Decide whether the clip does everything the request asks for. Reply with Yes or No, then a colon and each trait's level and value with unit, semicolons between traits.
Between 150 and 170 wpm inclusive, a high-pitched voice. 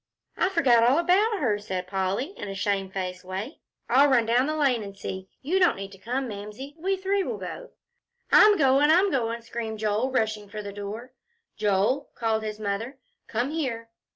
No: average, 185 wpm; high, 230 Hz